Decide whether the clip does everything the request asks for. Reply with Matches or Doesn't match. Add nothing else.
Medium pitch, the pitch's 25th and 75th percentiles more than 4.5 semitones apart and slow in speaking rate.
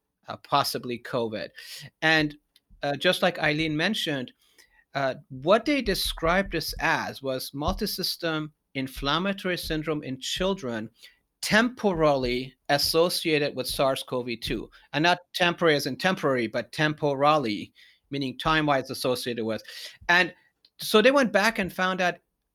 Matches